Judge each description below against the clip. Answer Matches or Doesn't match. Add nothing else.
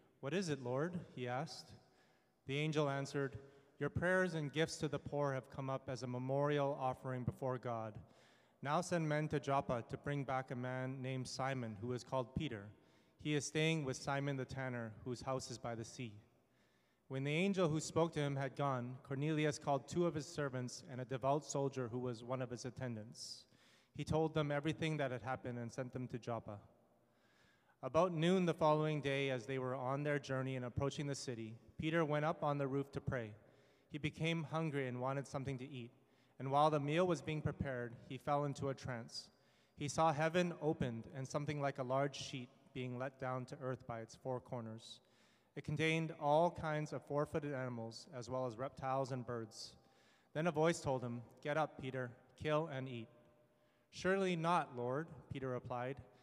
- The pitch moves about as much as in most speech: Matches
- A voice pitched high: Doesn't match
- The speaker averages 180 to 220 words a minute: Matches